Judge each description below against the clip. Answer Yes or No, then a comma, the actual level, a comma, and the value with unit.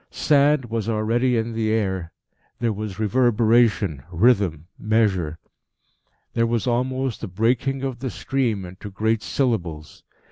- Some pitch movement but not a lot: Yes, average, 3.5 semitones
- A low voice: Yes, low, 115 Hz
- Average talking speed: No, slow, 130 wpm